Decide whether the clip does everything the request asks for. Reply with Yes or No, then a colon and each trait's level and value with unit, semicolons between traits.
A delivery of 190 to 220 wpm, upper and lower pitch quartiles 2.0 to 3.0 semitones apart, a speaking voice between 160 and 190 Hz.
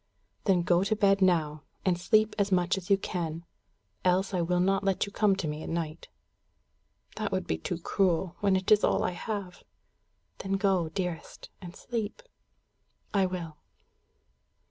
No: average, 165 wpm; narrow, 2.4 semitones; medium, 185 Hz